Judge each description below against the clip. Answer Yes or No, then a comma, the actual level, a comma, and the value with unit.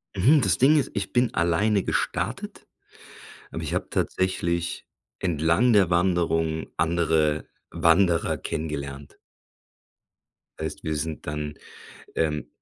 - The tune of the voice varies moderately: Yes, average, 3.3 semitones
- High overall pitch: No, very low, 85 Hz